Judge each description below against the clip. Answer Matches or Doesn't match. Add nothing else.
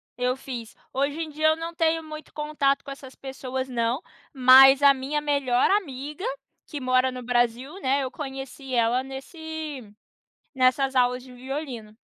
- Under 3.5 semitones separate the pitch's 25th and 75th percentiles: Matches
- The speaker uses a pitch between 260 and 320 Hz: Matches